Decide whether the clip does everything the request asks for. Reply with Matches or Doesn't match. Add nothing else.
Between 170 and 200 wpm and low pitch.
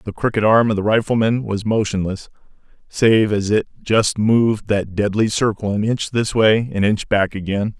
Matches